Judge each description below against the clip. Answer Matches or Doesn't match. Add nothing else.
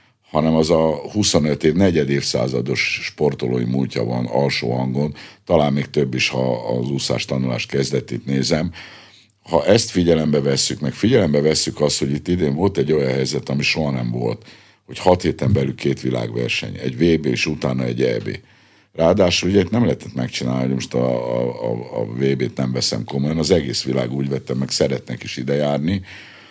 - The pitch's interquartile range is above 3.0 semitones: Matches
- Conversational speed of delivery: Doesn't match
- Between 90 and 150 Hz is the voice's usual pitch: Doesn't match